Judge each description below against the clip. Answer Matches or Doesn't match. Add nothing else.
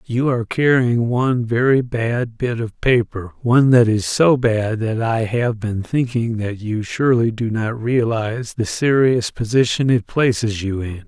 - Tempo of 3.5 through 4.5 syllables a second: Matches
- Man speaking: Matches